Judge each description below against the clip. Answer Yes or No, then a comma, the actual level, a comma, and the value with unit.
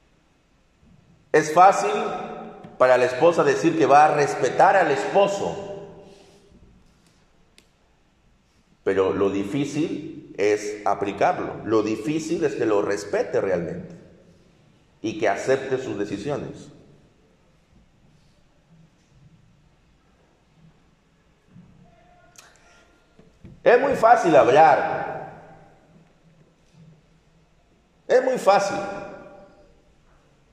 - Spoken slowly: Yes, slow, 70 wpm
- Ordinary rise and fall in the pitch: Yes, average, 4.9 semitones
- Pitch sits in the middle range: Yes, medium, 165 Hz